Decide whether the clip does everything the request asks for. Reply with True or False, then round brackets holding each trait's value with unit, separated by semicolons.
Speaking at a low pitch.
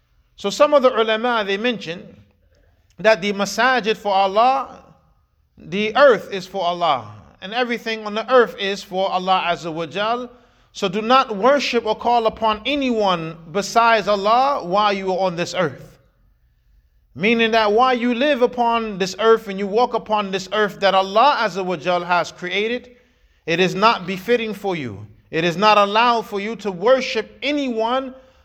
False (210 Hz)